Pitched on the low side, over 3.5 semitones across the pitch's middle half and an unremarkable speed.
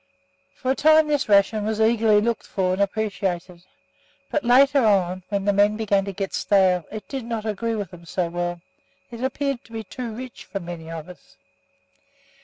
No: high, 210 Hz; average, 3.9 semitones; average, 190 wpm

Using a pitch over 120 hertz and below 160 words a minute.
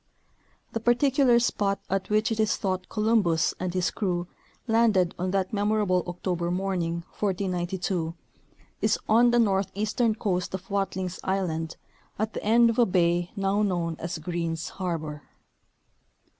Yes: high, 190 Hz; average, 140 wpm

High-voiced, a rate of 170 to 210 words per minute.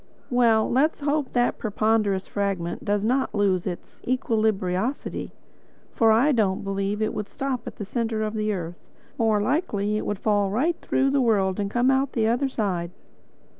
Yes: high, 215 Hz; average, 175 wpm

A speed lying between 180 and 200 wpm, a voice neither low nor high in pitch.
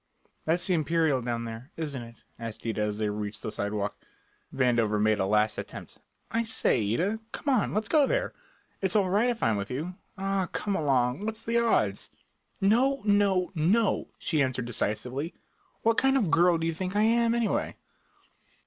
Yes: average, 185 wpm; medium, 165 Hz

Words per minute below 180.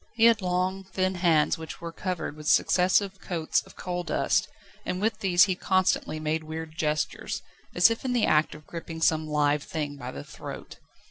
No: average, 190 wpm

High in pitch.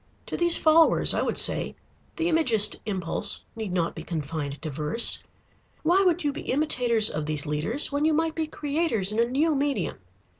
Yes: high, 240 Hz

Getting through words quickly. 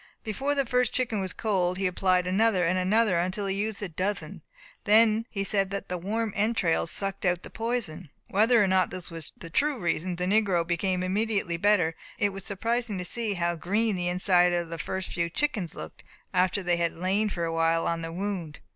Yes: fast, 215 wpm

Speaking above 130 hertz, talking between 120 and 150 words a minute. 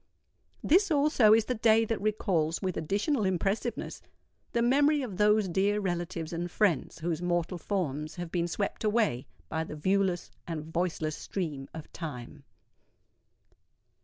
Yes: medium, 185 Hz; average, 140 wpm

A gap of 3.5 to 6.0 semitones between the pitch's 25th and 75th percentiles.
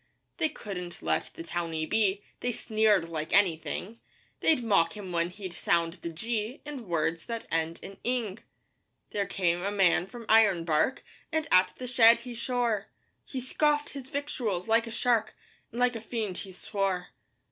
Yes: average, 5.3 semitones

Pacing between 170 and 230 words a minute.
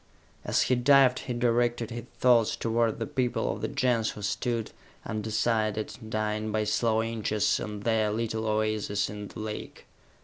No: average, 160 wpm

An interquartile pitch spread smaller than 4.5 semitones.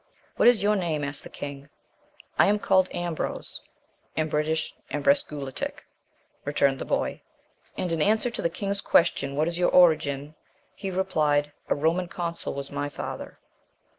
Yes: average, 3.9 semitones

